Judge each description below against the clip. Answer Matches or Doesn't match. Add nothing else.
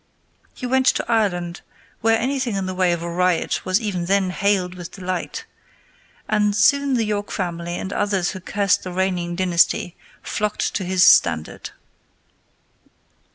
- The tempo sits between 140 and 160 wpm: Matches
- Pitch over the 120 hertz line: Matches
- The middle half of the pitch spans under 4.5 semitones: Matches